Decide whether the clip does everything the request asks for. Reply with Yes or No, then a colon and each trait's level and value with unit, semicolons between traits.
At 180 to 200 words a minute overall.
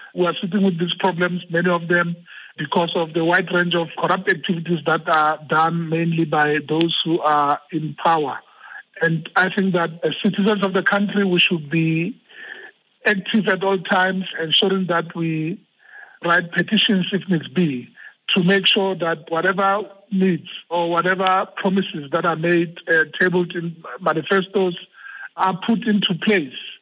No: average, 160 wpm